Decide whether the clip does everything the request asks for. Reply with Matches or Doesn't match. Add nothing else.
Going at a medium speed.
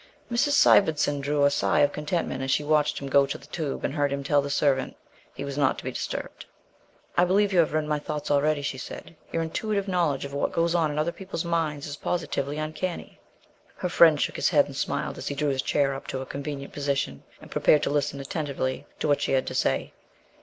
Doesn't match